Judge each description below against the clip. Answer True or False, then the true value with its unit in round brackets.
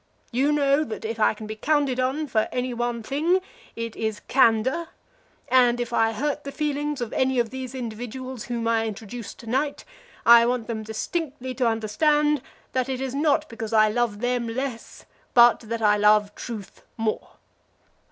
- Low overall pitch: False (240 Hz)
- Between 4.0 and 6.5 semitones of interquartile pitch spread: False (3.2 semitones)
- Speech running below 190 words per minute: True (175 wpm)